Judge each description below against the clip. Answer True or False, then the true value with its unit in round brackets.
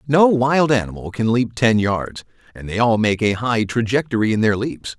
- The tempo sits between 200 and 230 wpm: True (205 wpm)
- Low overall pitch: True (115 Hz)